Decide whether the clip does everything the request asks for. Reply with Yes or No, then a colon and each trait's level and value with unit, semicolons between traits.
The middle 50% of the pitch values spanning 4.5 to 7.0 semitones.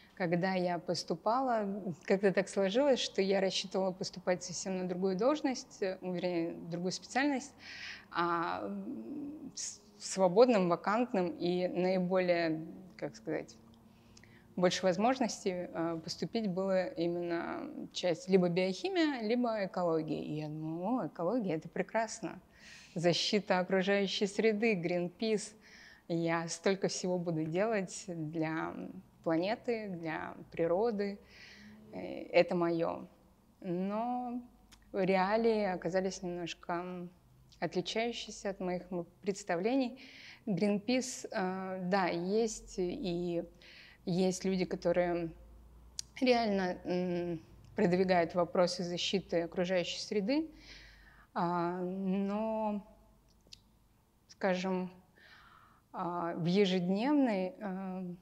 No: average, 3.3 semitones